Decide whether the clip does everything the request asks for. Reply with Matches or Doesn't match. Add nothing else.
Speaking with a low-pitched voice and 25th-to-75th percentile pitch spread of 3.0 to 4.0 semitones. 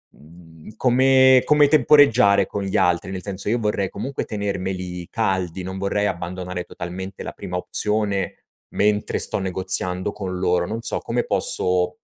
Doesn't match